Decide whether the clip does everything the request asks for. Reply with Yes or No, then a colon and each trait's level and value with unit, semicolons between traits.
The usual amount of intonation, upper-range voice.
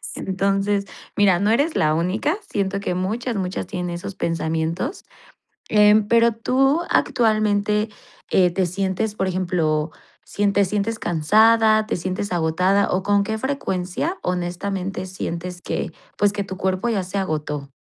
Yes: average, 3.0 semitones; high, 195 Hz